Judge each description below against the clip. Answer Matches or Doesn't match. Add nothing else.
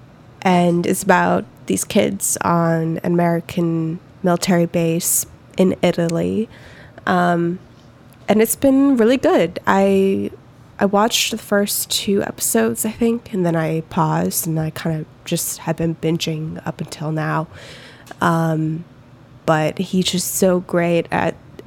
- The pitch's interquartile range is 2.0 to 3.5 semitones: Matches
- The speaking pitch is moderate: Matches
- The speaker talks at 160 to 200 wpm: Doesn't match